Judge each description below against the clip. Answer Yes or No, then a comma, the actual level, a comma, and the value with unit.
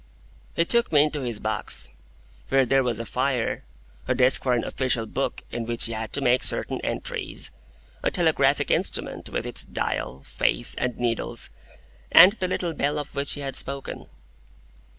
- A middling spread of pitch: Yes, average, 3.8 semitones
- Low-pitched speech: Yes, low, 130 Hz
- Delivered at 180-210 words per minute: No, average, 170 wpm